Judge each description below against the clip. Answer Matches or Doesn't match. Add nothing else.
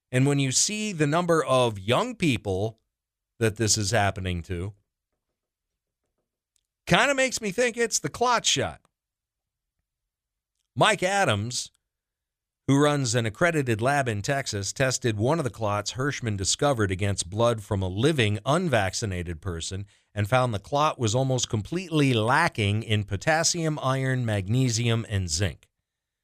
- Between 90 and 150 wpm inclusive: Matches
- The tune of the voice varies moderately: Doesn't match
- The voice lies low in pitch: Matches